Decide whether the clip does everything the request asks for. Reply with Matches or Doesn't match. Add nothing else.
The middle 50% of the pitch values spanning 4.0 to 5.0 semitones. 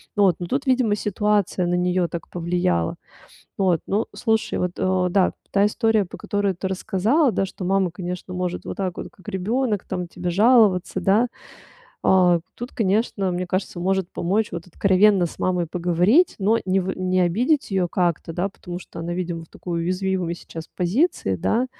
Doesn't match